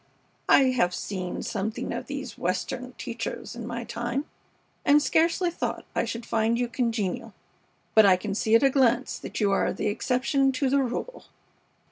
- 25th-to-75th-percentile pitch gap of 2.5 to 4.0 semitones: Yes, average, 3.4 semitones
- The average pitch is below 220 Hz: No, high, 235 Hz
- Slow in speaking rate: No, average, 170 wpm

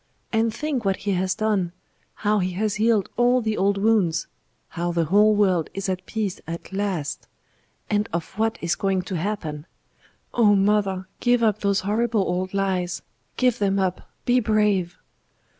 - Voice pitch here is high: Yes, high, 200 Hz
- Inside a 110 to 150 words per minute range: No, average, 165 wpm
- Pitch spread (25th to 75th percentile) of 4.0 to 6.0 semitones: No, average, 2.8 semitones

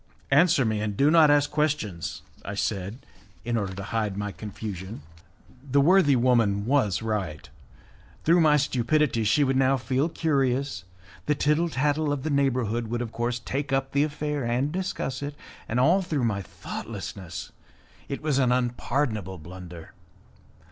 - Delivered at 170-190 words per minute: No, average, 155 wpm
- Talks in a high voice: No, low, 130 Hz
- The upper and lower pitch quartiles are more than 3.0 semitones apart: Yes, wide, 5.5 semitones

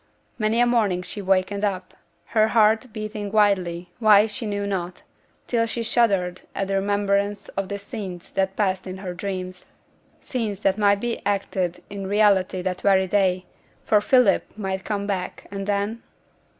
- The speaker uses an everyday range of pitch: No, narrow, 2.1 semitones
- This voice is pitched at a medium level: No, high, 200 Hz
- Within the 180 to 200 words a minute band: No, average, 165 wpm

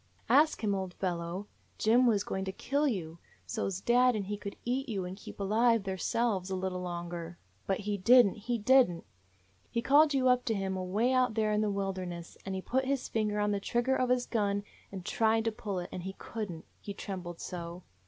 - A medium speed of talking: No, fast, 220 wpm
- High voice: Yes, high, 205 Hz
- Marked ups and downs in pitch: No, average, 4.2 semitones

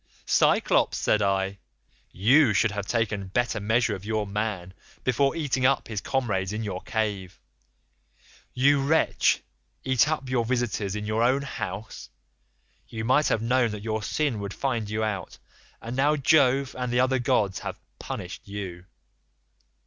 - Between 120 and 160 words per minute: Yes, average, 155 wpm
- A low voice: Yes, low, 110 Hz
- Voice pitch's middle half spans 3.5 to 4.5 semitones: Yes, average, 4.0 semitones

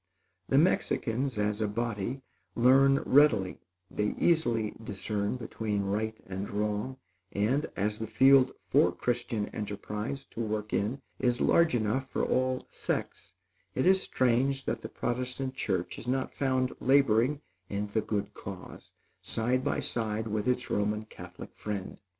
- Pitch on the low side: Yes, low, 115 Hz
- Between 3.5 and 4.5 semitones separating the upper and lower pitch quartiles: Yes, average, 3.8 semitones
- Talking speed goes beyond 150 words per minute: No, average, 145 wpm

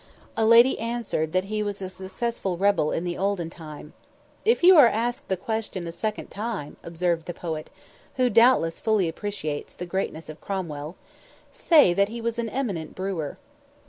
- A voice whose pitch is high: Yes, high, 195 Hz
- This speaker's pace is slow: No, average, 175 wpm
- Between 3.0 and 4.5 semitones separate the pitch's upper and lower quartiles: No, average, 5.2 semitones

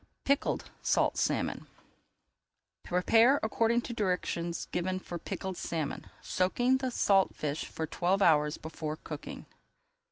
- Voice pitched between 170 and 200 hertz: Yes, medium, 185 Hz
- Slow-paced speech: Yes, slow, 120 wpm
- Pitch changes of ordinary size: No, wide, 5.8 semitones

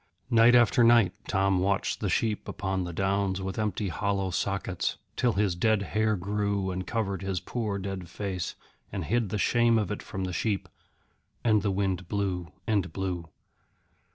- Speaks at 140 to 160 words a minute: No, average, 170 wpm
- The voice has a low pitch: Yes, low, 100 Hz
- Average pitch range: No, narrow, 2.3 semitones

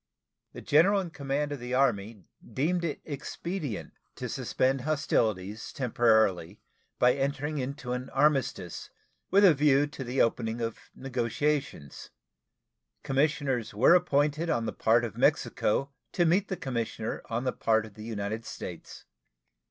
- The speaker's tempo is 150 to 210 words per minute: No, average, 140 wpm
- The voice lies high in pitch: No, low, 135 Hz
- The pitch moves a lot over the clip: No, average, 4.5 semitones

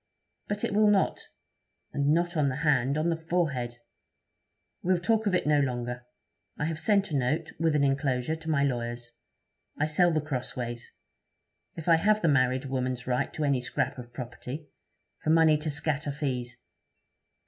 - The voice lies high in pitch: No, medium, 145 Hz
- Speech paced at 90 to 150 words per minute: No, average, 170 wpm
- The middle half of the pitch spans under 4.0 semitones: No, average, 4.3 semitones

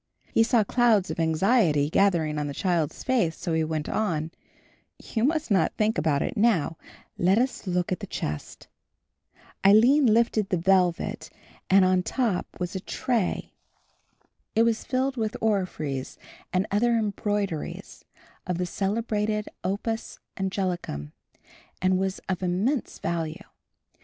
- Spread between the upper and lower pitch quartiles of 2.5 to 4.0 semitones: No, average, 4.5 semitones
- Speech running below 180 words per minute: Yes, average, 140 wpm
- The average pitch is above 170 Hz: Yes, high, 190 Hz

